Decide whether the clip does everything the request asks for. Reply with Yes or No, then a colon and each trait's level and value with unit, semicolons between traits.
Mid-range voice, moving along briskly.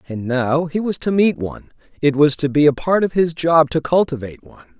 Yes: medium, 150 Hz; fast, 240 wpm